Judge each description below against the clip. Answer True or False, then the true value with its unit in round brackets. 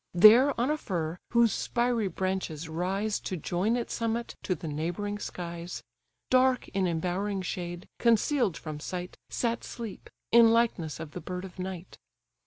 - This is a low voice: False (190 Hz)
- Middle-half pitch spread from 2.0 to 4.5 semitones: False (4.9 semitones)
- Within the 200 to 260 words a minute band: False (155 wpm)